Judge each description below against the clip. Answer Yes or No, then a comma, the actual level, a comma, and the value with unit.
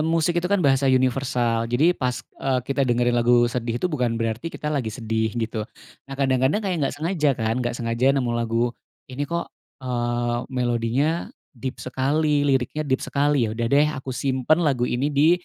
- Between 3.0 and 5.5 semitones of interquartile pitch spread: Yes, average, 3.4 semitones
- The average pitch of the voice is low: Yes, low, 130 Hz